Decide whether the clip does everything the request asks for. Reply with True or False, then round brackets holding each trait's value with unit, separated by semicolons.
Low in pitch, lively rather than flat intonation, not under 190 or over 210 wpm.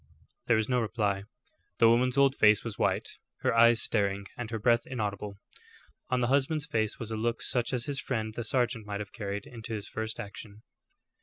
False (115 Hz; 2.6 semitones; 200 wpm)